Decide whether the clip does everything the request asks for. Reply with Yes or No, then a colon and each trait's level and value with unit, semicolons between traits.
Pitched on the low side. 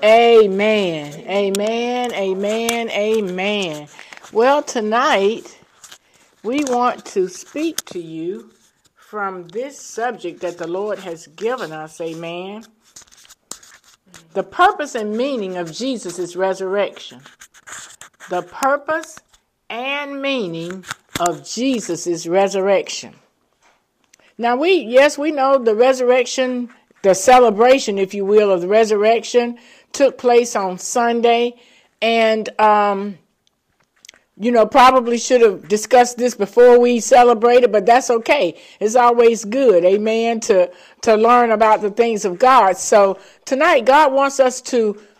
No: high, 225 Hz